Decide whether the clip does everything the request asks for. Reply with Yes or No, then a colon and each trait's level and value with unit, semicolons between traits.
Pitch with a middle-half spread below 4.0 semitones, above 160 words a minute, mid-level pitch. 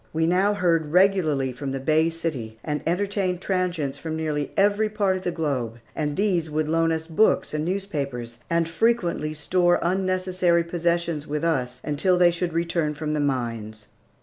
Yes: average, 3.6 semitones; average, 170 wpm; medium, 165 Hz